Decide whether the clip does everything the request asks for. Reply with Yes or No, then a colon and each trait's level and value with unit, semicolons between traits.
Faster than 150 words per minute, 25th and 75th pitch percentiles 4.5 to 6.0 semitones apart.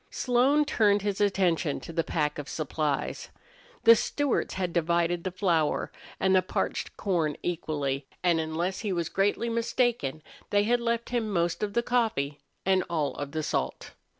Yes: average, 165 wpm; wide, 5.5 semitones